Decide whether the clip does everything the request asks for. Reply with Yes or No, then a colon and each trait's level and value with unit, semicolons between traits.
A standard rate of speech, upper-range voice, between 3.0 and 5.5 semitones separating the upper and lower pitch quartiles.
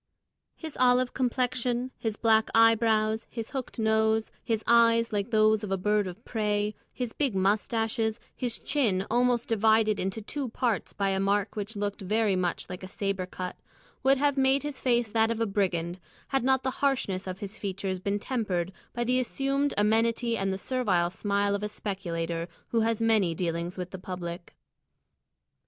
Yes: average, 175 wpm; high, 220 Hz; average, 3.6 semitones